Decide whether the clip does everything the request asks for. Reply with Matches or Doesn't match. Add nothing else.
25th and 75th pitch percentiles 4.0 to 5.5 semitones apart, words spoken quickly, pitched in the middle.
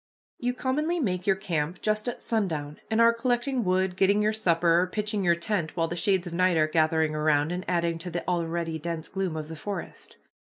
Matches